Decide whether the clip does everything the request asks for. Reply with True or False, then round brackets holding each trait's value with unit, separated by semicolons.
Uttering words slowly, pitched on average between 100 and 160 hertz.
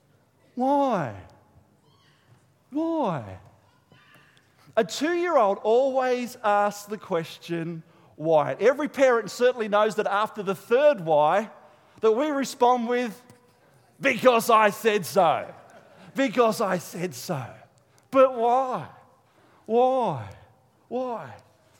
False (95 wpm; 205 Hz)